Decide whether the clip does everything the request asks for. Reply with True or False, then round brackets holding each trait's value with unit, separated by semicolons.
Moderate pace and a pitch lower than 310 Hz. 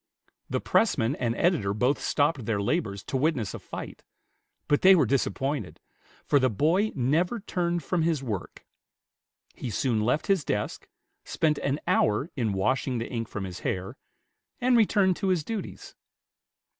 True (155 wpm; 135 Hz)